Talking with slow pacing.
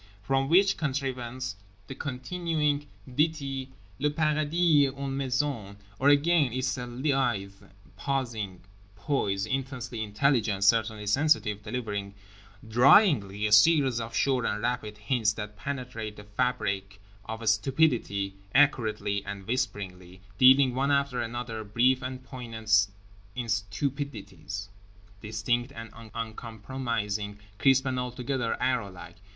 Yes: slow, 110 wpm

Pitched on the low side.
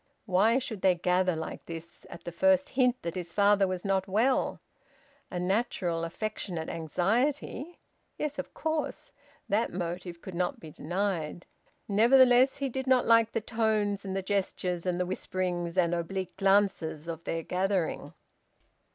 No: high, 190 Hz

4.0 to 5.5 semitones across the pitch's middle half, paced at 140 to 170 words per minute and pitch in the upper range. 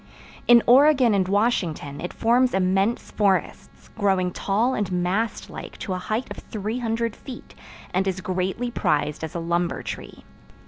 Yes: average, 4.3 semitones; average, 150 wpm; high, 200 Hz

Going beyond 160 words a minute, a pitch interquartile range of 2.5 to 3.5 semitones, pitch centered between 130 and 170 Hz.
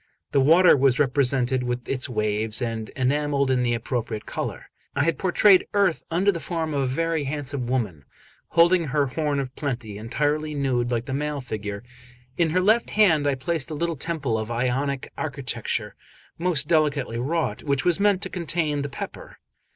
No: average, 175 wpm; average, 4.5 semitones; medium, 140 Hz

